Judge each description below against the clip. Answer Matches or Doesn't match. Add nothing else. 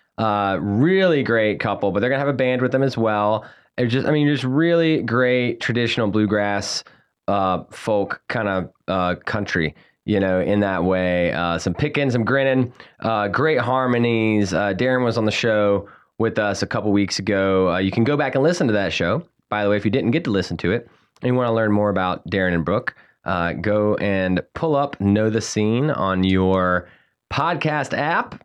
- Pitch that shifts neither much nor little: Matches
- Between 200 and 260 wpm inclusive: Matches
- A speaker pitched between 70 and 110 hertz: Matches